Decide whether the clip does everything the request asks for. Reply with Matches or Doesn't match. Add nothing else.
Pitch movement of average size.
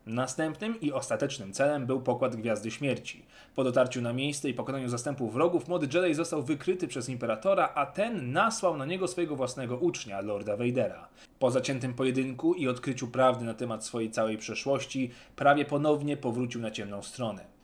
Matches